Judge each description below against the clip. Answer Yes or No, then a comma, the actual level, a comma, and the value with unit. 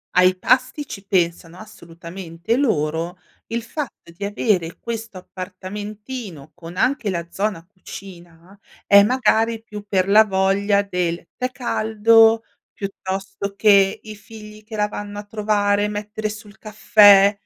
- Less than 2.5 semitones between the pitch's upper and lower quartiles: No, average, 2.8 semitones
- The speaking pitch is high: Yes, high, 205 Hz